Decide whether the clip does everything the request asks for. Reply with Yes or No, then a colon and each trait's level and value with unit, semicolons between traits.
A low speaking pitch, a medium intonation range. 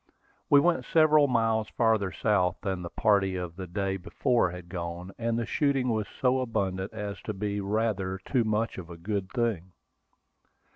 Yes: low, 105 Hz; average, 3.7 semitones